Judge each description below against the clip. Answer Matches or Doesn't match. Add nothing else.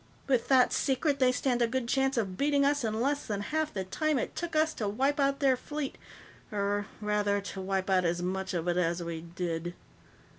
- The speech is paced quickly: Matches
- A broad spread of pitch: Matches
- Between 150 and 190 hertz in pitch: Doesn't match